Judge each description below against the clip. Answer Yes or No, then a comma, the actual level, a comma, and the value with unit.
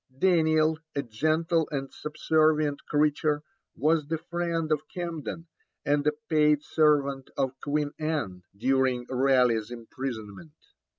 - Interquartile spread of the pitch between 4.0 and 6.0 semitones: No, average, 2.7 semitones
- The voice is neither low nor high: Yes, medium, 150 Hz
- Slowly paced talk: Yes, slow, 115 wpm